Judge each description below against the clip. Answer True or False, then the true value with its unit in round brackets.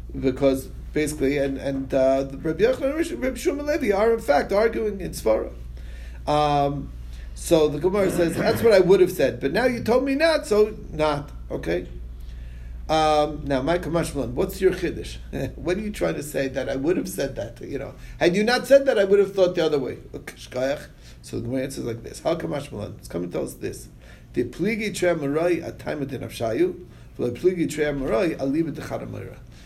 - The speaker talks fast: False (175 wpm)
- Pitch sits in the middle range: True (150 Hz)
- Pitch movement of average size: False (8.0 semitones)